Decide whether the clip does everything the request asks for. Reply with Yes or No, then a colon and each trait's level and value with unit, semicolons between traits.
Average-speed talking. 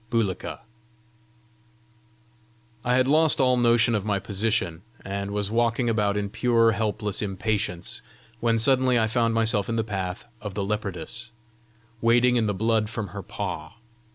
Yes: average, 150 wpm